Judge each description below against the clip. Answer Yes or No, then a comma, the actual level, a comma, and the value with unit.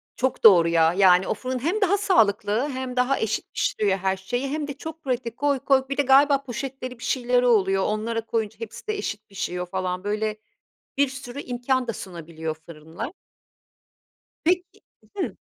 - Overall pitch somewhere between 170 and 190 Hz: No, high, 240 Hz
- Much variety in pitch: Yes, wide, 5.7 semitones